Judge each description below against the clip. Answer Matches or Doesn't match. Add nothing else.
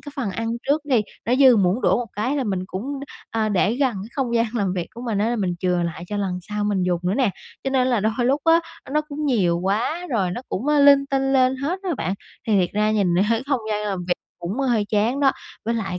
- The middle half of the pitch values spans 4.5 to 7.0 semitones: Matches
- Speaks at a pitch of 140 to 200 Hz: Doesn't match